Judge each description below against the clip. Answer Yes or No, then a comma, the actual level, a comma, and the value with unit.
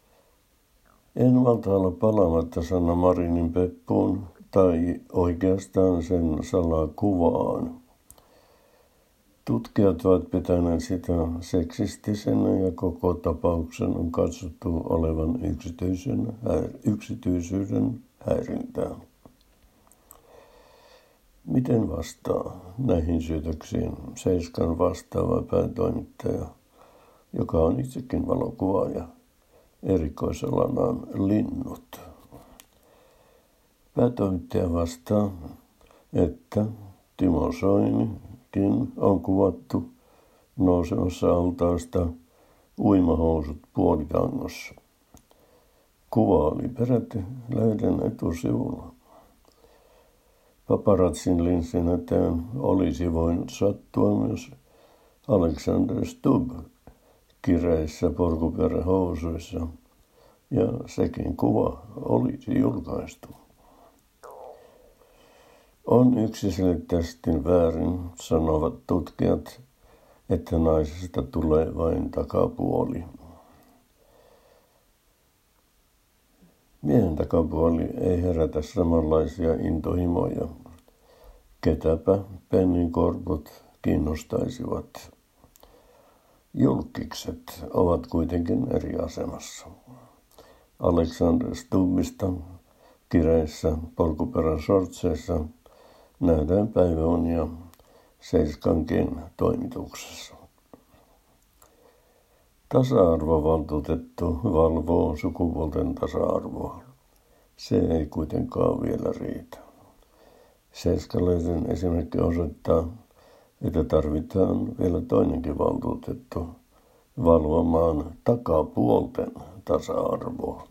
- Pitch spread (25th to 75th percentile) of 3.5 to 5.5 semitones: No, average, 2.9 semitones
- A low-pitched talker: Yes, very low, 90 Hz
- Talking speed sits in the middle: No, slow, 60 wpm